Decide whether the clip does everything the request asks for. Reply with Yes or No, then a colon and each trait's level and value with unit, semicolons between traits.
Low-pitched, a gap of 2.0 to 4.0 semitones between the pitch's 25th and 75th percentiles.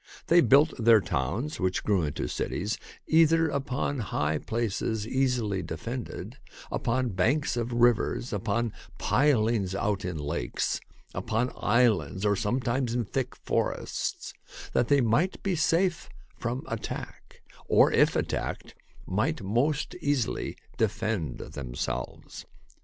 No: low, 115 Hz; average, 4.7 semitones